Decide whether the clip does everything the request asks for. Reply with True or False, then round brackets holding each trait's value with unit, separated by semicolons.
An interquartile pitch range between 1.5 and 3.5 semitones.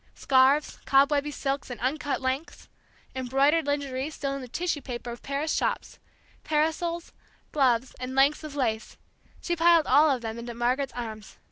True (3.0 semitones)